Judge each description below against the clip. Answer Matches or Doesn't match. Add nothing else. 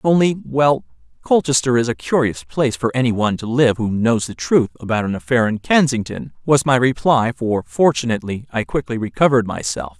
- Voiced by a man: Matches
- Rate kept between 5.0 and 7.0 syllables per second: Matches